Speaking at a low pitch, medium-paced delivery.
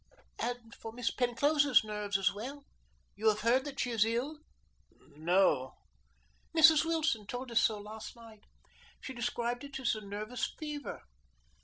No: high, 235 Hz; average, 150 wpm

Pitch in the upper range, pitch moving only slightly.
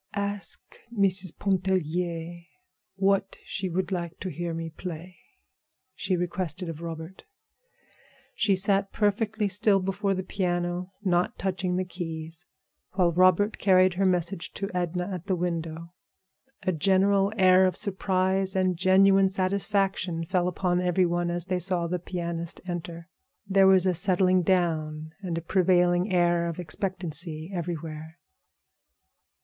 No: medium, 180 Hz; narrow, 2.0 semitones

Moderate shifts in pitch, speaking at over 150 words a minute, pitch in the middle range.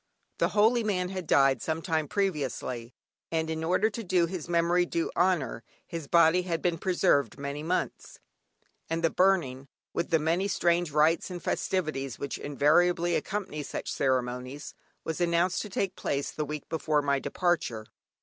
Yes: average, 3.8 semitones; average, 160 wpm; medium, 165 Hz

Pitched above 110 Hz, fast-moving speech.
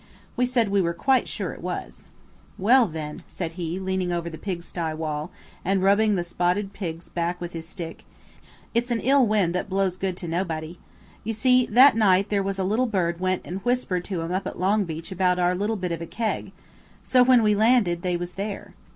Yes: medium, 185 Hz; fast, 210 wpm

